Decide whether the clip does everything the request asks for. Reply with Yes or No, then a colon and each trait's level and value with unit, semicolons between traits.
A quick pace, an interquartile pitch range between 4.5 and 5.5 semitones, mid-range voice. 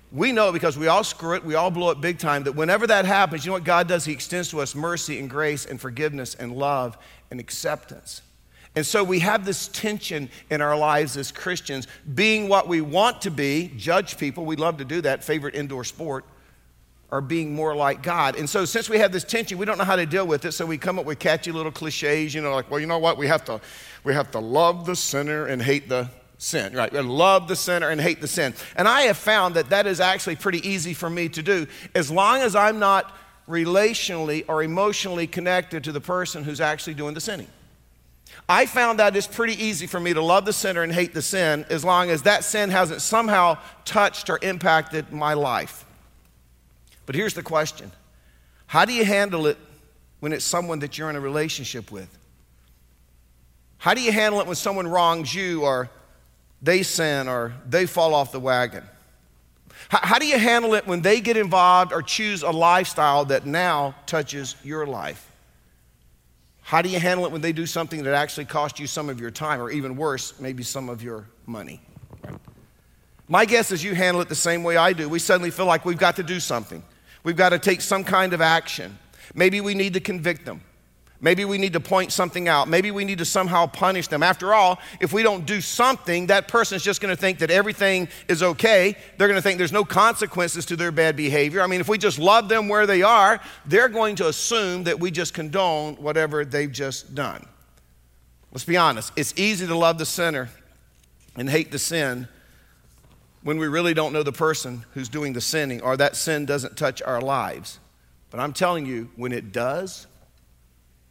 Yes: fast, 210 wpm; average, 5.0 semitones; medium, 165 Hz